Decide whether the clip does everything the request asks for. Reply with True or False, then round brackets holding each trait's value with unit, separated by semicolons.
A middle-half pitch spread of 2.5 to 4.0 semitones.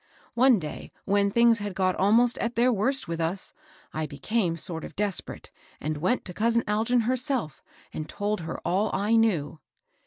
False (5.4 semitones)